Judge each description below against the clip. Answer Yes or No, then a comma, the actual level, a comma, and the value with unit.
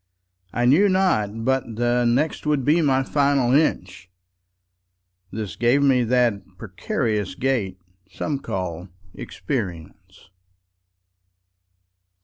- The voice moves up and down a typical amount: No, wide, 6.4 semitones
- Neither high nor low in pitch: No, low, 115 Hz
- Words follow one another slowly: Yes, slow, 85 wpm